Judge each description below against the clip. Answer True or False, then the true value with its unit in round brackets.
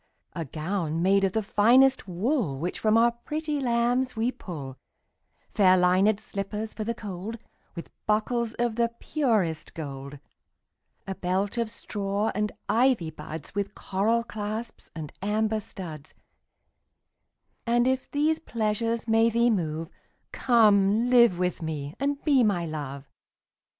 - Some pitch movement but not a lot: True (4.7 semitones)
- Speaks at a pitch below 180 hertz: False (210 Hz)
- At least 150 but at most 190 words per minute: False (140 wpm)